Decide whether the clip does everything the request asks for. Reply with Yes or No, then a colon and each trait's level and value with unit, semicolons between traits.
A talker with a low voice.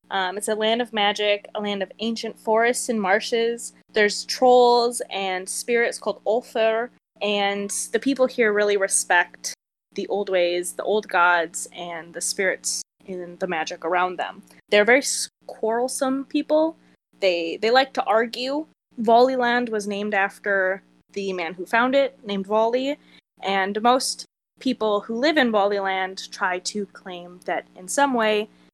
No: high, 210 Hz